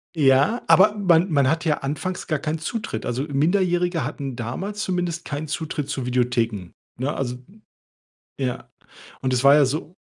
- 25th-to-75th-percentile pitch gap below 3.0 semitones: No, average, 4.9 semitones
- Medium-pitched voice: Yes, medium, 150 Hz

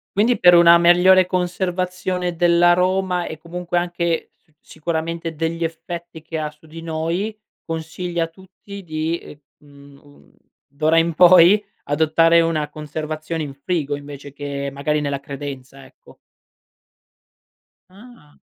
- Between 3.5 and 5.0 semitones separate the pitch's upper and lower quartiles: No, average, 2.7 semitones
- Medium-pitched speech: Yes, medium, 165 Hz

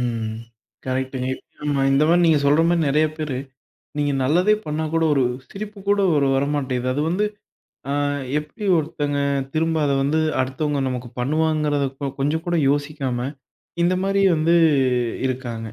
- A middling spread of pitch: Yes, average, 3.4 semitones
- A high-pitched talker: No, medium, 145 Hz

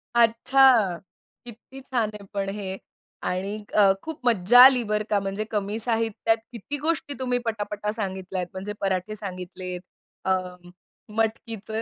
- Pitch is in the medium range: No, high, 210 Hz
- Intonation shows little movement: No, average, 3.2 semitones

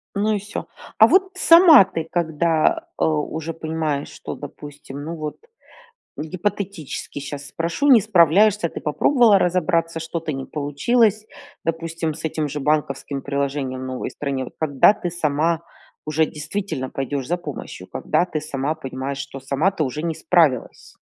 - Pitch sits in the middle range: Yes, medium, 160 Hz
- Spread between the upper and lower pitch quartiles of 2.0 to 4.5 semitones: Yes, average, 3.8 semitones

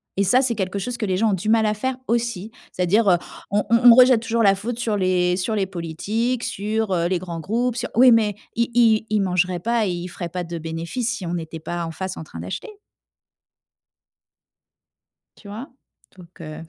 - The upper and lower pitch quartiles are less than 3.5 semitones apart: No, average, 4.4 semitones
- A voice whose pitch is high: Yes, high, 200 Hz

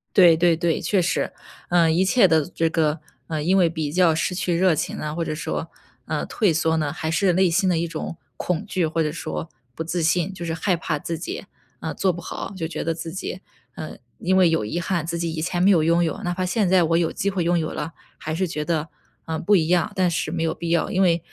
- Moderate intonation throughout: No, narrow, 1.9 semitones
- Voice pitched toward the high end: No, medium, 170 Hz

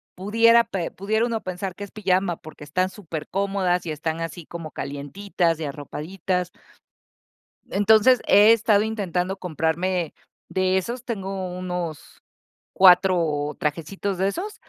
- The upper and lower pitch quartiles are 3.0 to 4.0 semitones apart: Yes, average, 3.4 semitones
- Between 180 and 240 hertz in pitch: Yes, medium, 185 Hz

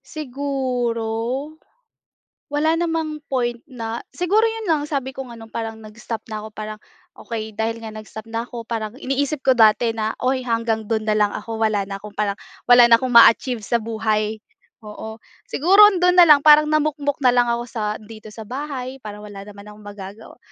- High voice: Yes, high, 230 Hz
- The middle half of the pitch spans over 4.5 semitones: No, average, 4.0 semitones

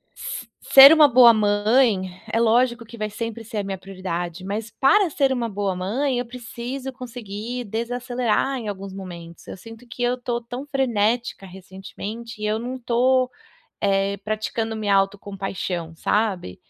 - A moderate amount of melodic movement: Yes, average, 3.9 semitones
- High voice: Yes, high, 225 Hz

